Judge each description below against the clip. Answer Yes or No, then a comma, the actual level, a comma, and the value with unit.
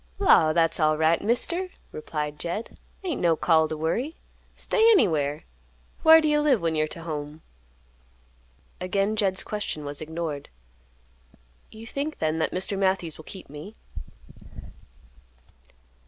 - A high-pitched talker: No, medium, 170 Hz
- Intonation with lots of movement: Yes, wide, 6.1 semitones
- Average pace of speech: No, slow, 130 wpm